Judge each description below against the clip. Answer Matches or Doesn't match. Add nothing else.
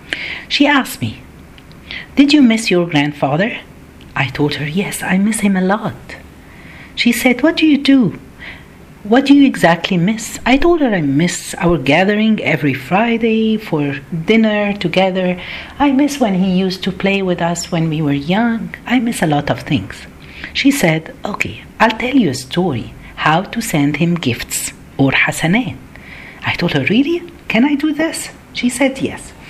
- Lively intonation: Matches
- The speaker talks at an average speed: Doesn't match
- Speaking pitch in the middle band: Doesn't match